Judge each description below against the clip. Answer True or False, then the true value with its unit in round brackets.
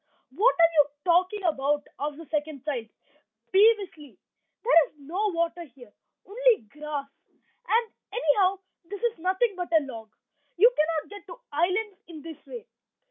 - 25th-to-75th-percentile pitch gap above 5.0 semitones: True (5.6 semitones)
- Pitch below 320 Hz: False (335 Hz)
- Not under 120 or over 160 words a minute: True (150 wpm)